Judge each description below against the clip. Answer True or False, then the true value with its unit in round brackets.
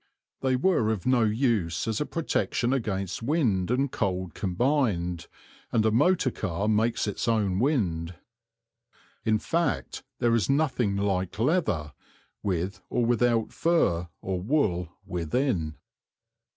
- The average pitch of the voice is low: True (110 Hz)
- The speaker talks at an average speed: False (125 wpm)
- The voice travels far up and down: True (5.9 semitones)